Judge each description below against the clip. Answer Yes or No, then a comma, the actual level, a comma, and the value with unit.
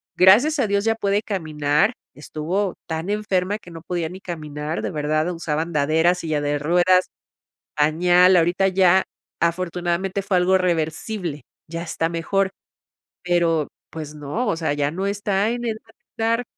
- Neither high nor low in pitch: Yes, medium, 175 Hz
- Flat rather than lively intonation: No, average, 3.7 semitones